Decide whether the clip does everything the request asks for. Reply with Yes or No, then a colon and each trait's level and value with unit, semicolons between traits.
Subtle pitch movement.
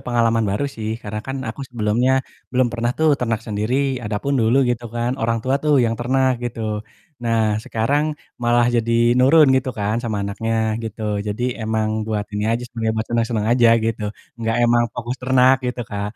Yes: narrow, 2.0 semitones